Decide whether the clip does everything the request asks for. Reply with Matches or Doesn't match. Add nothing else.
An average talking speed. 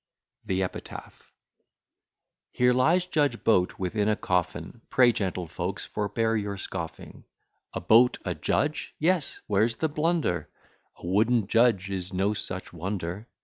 Doesn't match